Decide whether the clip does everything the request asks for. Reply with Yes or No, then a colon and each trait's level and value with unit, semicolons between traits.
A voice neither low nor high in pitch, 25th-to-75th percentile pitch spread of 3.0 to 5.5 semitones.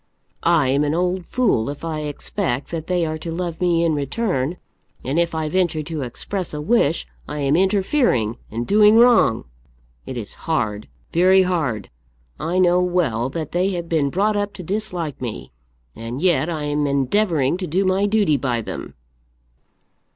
Yes: medium, 165 Hz; average, 4.7 semitones